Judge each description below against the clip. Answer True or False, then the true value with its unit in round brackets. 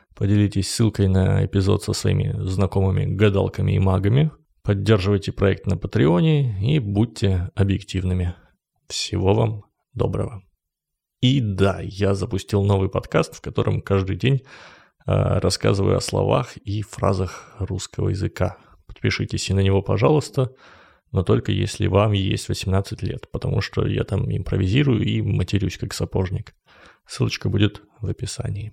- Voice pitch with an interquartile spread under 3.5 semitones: True (2.9 semitones)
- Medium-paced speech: True (130 wpm)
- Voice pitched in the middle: False (100 Hz)